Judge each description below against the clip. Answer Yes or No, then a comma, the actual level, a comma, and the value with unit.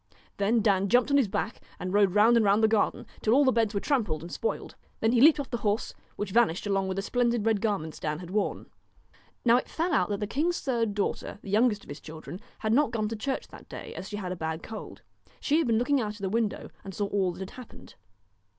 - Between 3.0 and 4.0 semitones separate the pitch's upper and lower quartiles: Yes, average, 3.4 semitones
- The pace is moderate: No, fast, 255 wpm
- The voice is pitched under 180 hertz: No, high, 215 Hz